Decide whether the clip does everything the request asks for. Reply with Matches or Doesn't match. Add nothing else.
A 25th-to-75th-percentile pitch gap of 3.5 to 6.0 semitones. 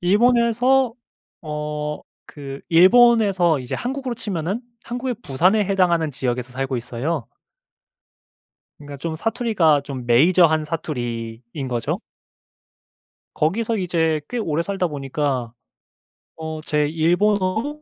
Doesn't match